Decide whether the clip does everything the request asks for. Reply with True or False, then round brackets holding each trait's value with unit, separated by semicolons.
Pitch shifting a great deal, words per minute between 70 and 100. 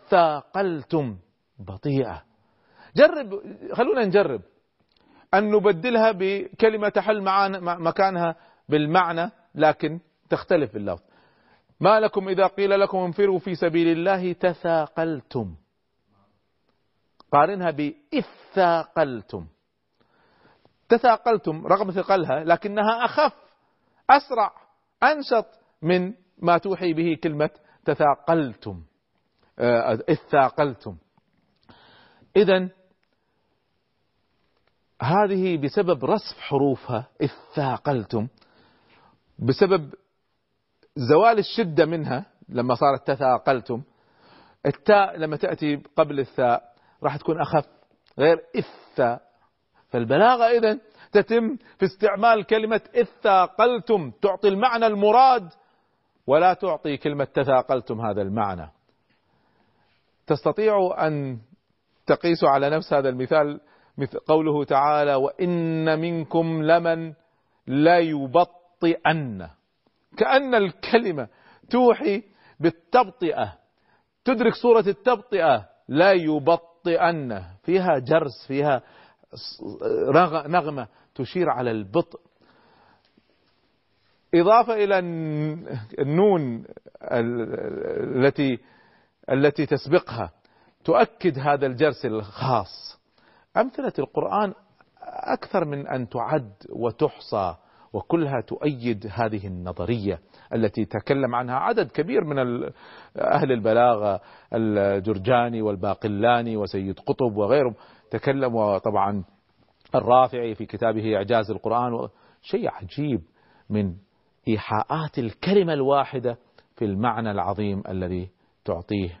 True (8.0 semitones; 80 wpm)